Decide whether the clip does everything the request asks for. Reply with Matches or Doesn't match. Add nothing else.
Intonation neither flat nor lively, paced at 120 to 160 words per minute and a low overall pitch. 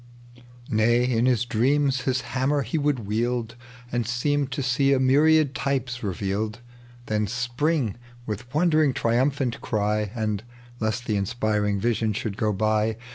Matches